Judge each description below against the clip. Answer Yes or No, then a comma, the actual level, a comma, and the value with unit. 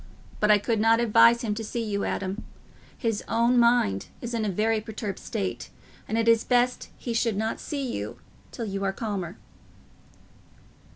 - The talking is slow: No, average, 175 wpm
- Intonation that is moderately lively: No, narrow, 2.3 semitones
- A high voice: Yes, high, 225 Hz